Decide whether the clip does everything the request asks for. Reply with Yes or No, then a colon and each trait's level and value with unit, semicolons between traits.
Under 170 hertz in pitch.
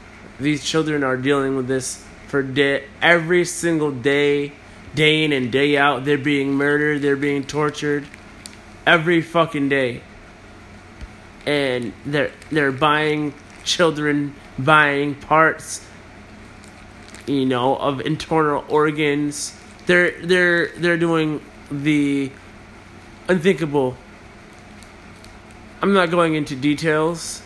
Yes: medium, 140 Hz